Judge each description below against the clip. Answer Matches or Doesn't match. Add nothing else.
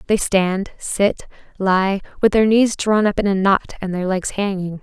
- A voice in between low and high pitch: Doesn't match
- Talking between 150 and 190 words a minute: Doesn't match